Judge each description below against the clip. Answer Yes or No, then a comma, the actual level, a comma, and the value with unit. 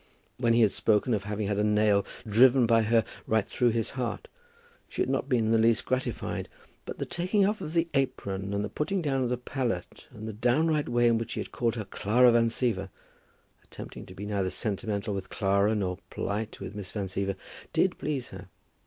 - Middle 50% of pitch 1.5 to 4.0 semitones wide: Yes, average, 3.5 semitones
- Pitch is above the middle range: No, low, 115 Hz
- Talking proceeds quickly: Yes, fast, 215 wpm